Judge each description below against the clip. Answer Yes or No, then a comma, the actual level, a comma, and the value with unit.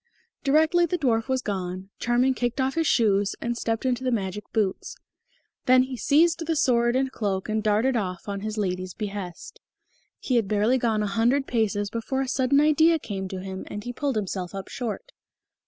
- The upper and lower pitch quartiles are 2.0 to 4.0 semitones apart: No, average, 4.6 semitones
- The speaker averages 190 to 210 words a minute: Yes, average, 195 wpm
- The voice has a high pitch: Yes, high, 230 Hz